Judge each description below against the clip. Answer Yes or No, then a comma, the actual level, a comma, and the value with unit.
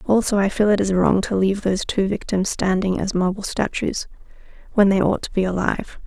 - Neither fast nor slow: No, fast, 210 wpm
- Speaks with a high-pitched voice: Yes, high, 195 Hz